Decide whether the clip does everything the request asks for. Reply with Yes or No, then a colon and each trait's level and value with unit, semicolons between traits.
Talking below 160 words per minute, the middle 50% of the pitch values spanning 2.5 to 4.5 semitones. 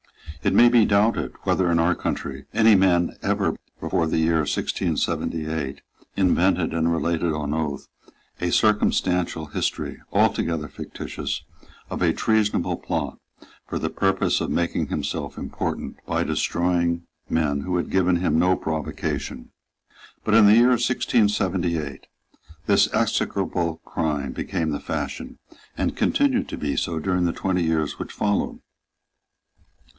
Yes: slow, 135 wpm; average, 3.2 semitones